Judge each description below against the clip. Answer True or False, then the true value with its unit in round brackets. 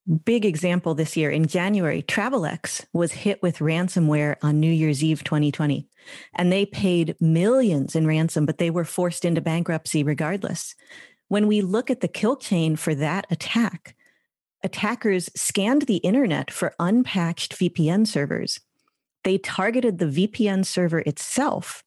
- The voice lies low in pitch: False (175 Hz)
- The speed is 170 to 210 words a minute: False (145 wpm)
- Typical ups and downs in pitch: True (4.1 semitones)